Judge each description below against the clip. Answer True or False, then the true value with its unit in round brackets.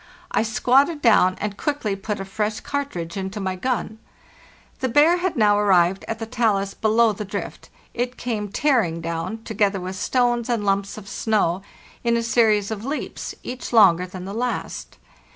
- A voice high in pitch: True (215 Hz)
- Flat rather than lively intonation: False (3.6 semitones)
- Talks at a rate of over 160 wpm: True (170 wpm)